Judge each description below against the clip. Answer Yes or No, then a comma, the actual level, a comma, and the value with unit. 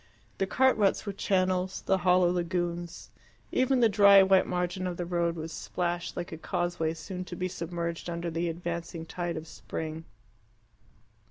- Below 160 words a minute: No, average, 165 wpm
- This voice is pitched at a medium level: Yes, medium, 175 Hz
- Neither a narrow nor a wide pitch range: No, narrow, 1.6 semitones